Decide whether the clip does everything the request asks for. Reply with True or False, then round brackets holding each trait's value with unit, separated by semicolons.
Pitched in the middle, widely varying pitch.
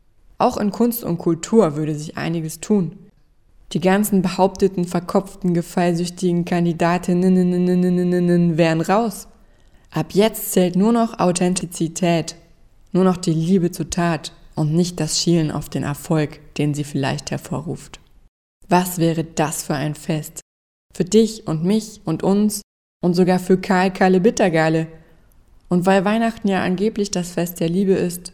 False (180 Hz; 3.0 semitones)